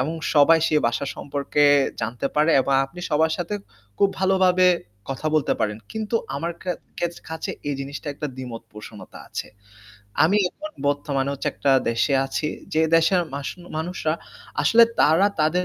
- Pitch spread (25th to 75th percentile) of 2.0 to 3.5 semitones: No, average, 4.3 semitones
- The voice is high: No, medium, 155 Hz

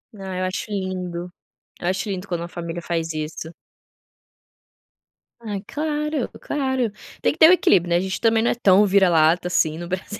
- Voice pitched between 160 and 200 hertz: Yes, medium, 185 Hz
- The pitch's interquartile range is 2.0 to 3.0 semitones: No, average, 3.8 semitones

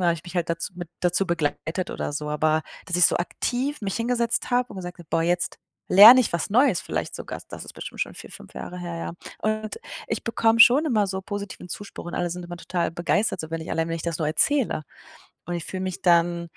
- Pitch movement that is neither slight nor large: Yes, average, 4.2 semitones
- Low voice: No, medium, 175 Hz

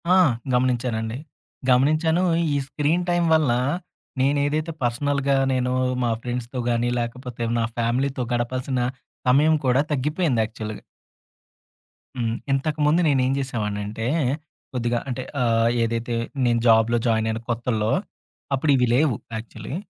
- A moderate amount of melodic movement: Yes, average, 3.4 semitones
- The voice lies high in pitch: No, low, 125 Hz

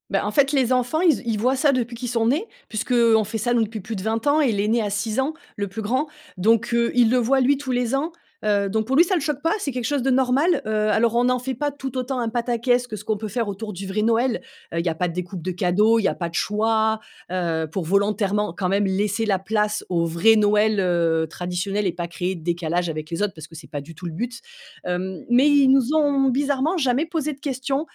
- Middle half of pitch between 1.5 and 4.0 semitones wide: No, average, 4.9 semitones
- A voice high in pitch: Yes, high, 225 Hz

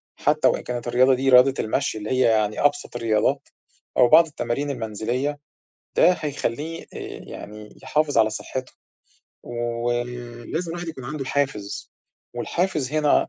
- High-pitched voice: No, low, 130 Hz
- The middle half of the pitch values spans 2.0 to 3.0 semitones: No, average, 3.9 semitones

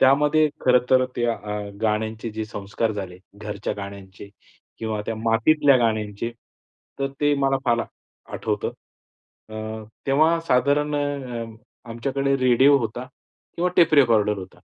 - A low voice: Yes, low, 115 Hz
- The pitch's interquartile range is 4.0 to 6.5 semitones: Yes, average, 4.4 semitones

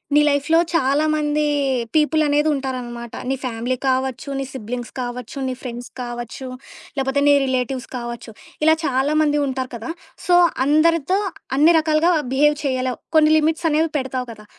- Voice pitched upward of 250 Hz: Yes, very high, 270 Hz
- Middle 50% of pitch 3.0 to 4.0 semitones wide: Yes, average, 3.4 semitones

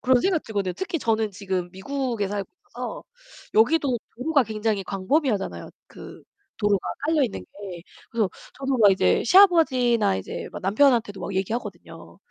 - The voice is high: Yes, high, 225 Hz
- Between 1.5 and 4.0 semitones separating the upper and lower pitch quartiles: No, wide, 5.5 semitones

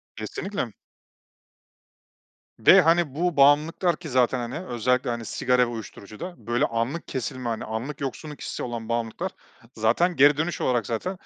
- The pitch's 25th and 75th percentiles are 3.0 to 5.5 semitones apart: Yes, average, 5.1 semitones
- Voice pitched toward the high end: No, low, 130 Hz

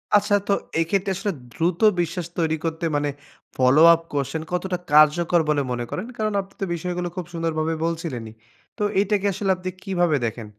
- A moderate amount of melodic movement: Yes, average, 3.5 semitones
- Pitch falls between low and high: Yes, medium, 170 Hz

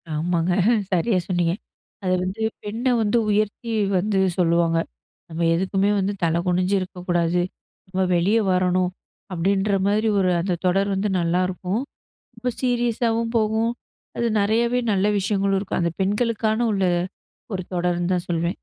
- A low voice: No, high, 190 Hz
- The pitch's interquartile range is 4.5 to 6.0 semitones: No, average, 3.2 semitones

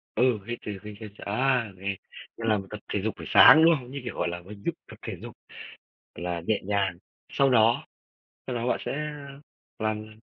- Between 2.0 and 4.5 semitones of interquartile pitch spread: Yes, average, 3.6 semitones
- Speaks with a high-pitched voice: No, low, 110 Hz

